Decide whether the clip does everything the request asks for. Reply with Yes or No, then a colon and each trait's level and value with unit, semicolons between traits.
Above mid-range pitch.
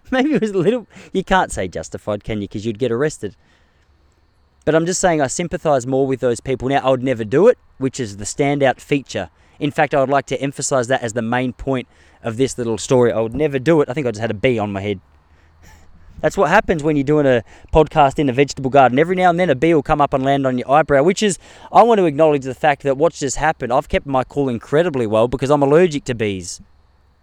No: low, 135 Hz